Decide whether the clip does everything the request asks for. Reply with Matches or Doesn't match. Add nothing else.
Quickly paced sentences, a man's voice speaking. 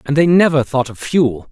Matches